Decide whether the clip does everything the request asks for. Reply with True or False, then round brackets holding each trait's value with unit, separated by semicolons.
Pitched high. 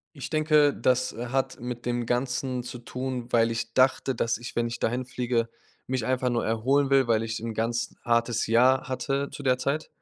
False (125 Hz)